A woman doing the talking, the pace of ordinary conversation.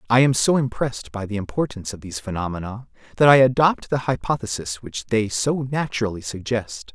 No: male; average, 175 wpm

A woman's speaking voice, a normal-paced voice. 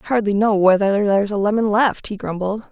No: female; fast, 220 wpm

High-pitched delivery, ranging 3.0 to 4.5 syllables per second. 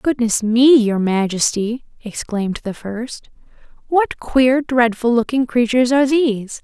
Yes: high, 240 Hz; 4.3 syllables/s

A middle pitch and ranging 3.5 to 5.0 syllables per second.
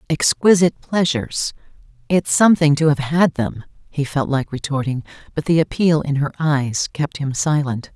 Yes: medium, 150 Hz; 4.9 syllables/s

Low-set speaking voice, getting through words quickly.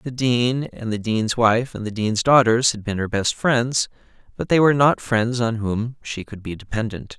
Yes: low, 115 Hz; fast, 215 wpm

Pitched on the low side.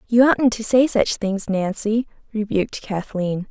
No: high, 215 Hz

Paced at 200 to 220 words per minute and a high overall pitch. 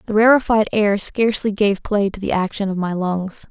Yes: fast, 205 wpm; high, 205 Hz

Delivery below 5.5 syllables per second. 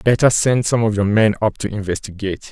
No: 5.8 syllables/s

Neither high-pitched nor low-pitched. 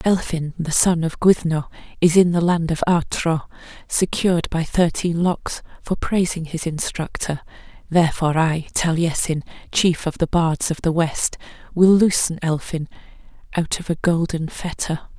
Yes: medium, 165 Hz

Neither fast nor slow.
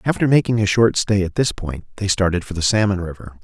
No: fast, 245 wpm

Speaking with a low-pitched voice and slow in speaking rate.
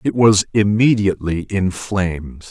Yes: very low, 95 Hz; slow, 120 wpm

